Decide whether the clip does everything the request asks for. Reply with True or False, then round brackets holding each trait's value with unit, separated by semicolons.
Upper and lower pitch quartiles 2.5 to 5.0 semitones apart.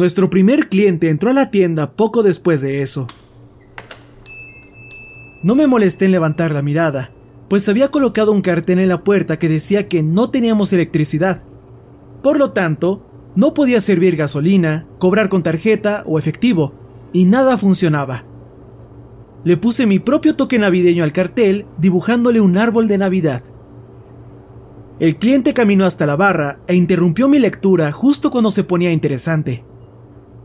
False (5.6 semitones)